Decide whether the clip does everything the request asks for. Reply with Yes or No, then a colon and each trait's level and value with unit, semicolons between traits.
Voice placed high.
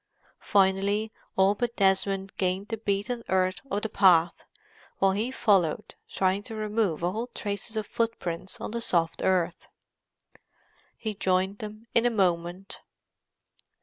Yes: high, 195 Hz